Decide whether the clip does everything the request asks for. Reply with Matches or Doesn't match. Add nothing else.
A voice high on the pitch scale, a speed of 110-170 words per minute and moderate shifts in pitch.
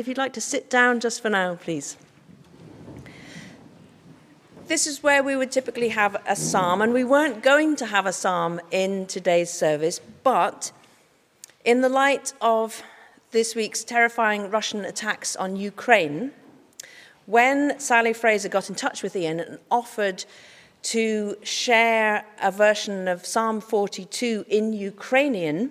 Matches